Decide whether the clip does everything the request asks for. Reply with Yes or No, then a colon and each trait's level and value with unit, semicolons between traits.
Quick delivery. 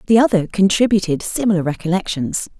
No: slow, 115 wpm